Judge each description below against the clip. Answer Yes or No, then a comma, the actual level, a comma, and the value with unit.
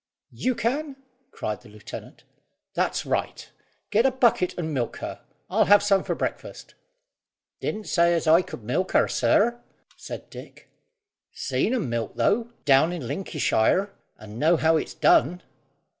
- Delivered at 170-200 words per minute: No, average, 145 wpm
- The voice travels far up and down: Yes, wide, 8.2 semitones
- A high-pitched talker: No, medium, 175 Hz